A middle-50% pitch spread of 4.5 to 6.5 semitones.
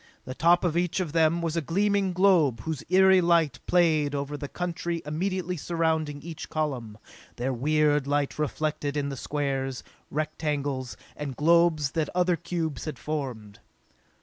No: average, 3.1 semitones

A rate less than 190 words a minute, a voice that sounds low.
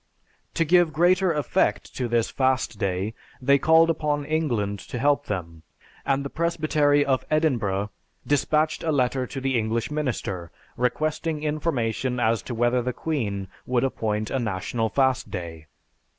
Yes: average, 150 wpm; low, 130 Hz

